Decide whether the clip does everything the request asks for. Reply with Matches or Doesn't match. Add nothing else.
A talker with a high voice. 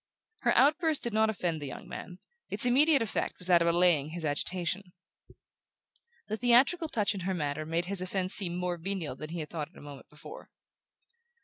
Doesn't match